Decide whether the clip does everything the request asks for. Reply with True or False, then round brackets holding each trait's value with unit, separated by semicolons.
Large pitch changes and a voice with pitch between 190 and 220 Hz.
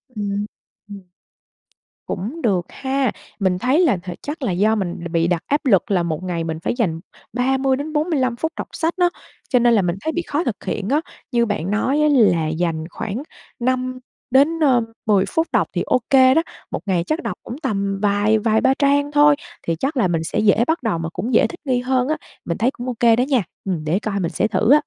False (6.2 semitones; 230 Hz)